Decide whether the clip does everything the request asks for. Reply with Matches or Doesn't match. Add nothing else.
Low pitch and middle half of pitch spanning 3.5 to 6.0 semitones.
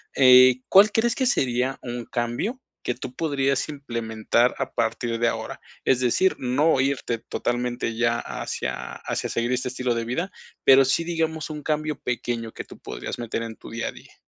Matches